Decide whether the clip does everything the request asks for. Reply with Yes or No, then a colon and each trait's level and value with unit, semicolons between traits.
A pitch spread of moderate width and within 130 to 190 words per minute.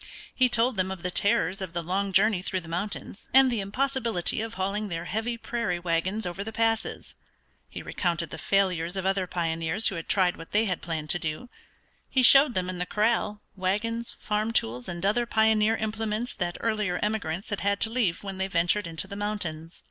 No: average, 3.9 semitones; average, 200 wpm